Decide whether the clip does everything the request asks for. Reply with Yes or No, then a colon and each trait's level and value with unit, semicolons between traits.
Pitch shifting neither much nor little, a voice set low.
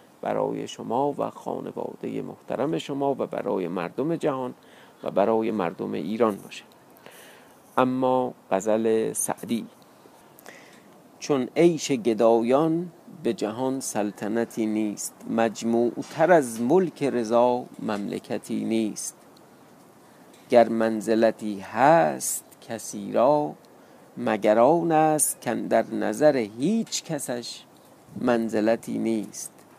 Yes: average, 3.8 semitones; low, 120 Hz